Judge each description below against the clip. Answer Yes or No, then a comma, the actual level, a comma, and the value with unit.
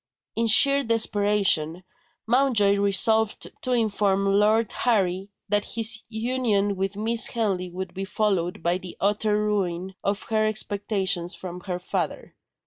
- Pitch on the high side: Yes, high, 205 Hz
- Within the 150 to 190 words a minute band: No, slow, 135 wpm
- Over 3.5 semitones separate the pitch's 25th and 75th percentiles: No, average, 2.7 semitones